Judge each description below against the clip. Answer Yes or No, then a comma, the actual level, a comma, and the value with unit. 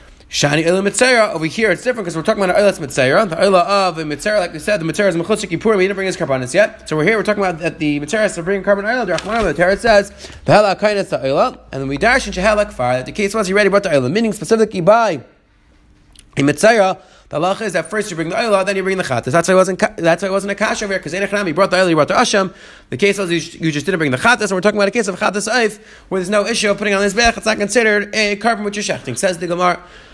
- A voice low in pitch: No, high, 195 Hz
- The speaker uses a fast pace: Yes, fast, 270 wpm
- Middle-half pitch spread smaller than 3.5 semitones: No, average, 3.8 semitones